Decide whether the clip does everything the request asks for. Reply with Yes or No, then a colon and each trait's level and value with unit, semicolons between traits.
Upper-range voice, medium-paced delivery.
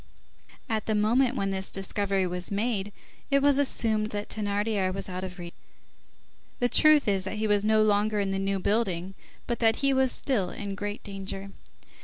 Yes: high, 205 Hz; average, 185 wpm